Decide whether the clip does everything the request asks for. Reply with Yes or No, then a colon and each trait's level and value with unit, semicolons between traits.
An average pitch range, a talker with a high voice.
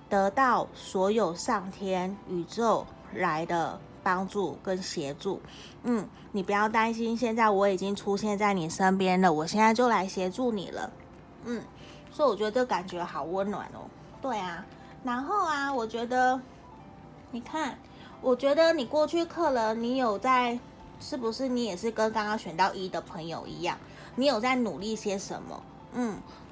Yes: average, 4.6 semitones; high, 215 Hz